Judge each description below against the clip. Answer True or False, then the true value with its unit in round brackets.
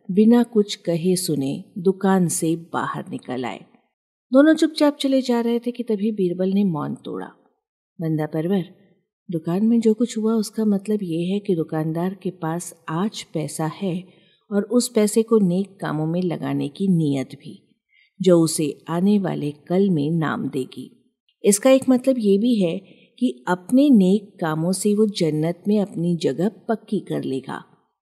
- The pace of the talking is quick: False (165 wpm)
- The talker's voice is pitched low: False (190 Hz)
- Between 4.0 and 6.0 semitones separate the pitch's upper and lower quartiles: True (4.8 semitones)